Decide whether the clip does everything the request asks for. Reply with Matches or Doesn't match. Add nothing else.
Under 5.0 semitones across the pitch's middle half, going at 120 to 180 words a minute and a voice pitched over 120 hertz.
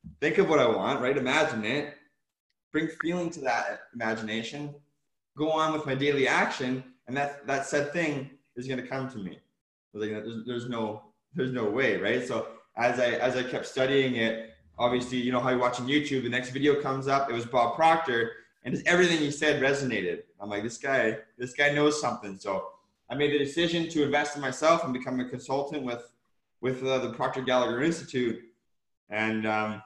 Doesn't match